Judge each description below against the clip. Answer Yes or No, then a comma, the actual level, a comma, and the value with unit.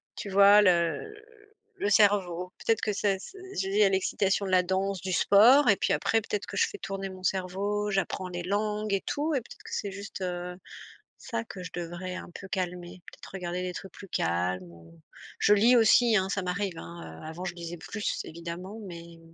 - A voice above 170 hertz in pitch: Yes, high, 190 Hz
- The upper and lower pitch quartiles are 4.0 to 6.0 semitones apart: No, average, 2.7 semitones